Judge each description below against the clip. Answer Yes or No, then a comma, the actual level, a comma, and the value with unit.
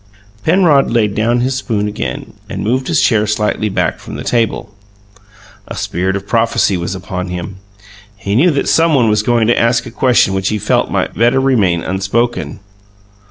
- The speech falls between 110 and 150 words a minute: No, average, 175 wpm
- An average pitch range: Yes, average, 3.9 semitones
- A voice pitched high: No, low, 110 Hz